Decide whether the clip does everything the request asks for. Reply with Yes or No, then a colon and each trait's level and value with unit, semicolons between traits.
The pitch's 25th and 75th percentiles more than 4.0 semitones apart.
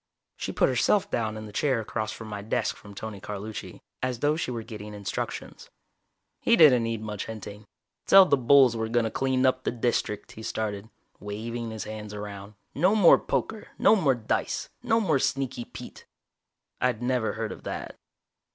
No: average, 3.6 semitones